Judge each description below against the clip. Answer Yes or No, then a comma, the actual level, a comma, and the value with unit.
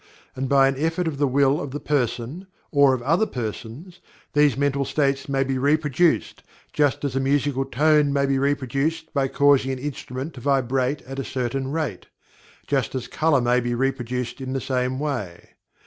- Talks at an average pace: Yes, average, 180 wpm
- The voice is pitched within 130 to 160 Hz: Yes, low, 135 Hz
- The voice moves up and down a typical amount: No, narrow, 2.0 semitones